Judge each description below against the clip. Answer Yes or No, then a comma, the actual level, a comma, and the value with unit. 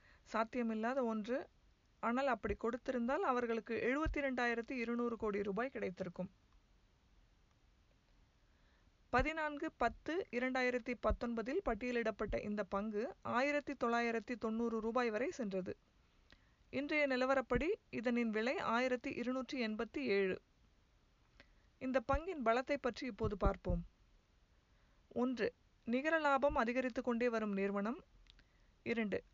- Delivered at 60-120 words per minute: Yes, average, 95 wpm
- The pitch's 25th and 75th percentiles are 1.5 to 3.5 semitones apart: Yes, average, 2.8 semitones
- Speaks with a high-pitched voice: Yes, high, 245 Hz